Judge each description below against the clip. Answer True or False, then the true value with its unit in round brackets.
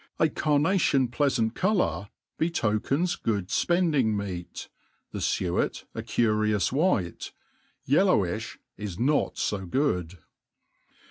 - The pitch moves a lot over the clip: True (6.9 semitones)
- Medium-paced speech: False (105 wpm)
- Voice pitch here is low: True (120 Hz)